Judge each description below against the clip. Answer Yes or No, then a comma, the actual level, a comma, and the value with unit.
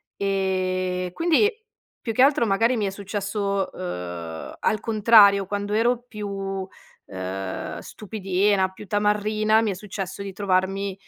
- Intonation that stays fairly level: Yes, narrow, 2.2 semitones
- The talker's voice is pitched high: Yes, high, 200 Hz